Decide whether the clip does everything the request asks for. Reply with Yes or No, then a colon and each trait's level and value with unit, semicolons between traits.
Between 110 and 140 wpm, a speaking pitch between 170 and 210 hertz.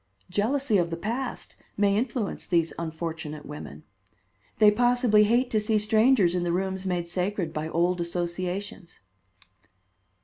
Yes: slow, 135 wpm; high, 190 Hz